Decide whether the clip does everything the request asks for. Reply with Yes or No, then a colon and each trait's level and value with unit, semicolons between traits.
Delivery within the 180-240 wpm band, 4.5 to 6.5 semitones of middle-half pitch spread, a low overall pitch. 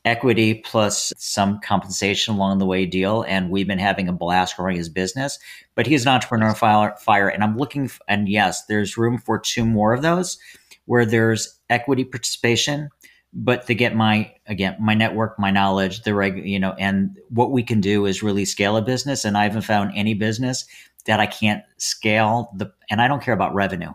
No: average, 200 wpm; average, 3.2 semitones; low, 110 Hz